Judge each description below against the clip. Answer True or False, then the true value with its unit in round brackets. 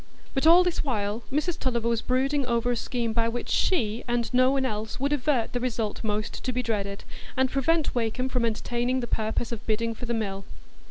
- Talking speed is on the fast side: True (210 wpm)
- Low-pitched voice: False (240 Hz)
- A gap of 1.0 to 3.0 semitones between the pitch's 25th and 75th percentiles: True (2.6 semitones)